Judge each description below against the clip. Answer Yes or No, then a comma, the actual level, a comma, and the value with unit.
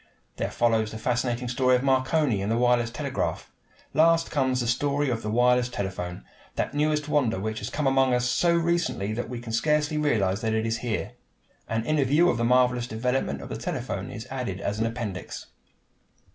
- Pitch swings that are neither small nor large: Yes, average, 3.7 semitones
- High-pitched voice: No, low, 125 Hz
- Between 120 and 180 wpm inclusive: No, average, 195 wpm